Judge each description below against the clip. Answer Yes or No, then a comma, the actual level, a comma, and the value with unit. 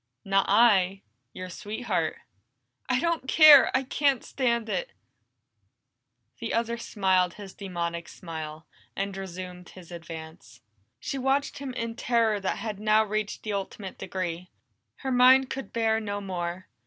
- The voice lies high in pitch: Yes, high, 205 Hz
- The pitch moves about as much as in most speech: Yes, average, 4.6 semitones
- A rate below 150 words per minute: Yes, average, 140 wpm